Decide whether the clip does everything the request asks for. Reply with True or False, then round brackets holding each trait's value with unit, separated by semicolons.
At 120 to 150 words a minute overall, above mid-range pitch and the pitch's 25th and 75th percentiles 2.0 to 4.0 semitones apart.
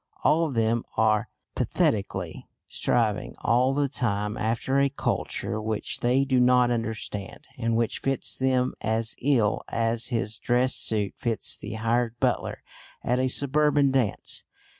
False (140 wpm; 120 Hz; 2.8 semitones)